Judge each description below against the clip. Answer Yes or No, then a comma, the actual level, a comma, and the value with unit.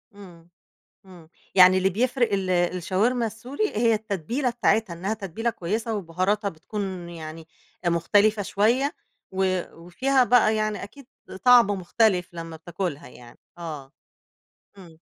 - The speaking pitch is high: Yes, high, 195 Hz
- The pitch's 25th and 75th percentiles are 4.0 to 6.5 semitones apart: Yes, average, 4.4 semitones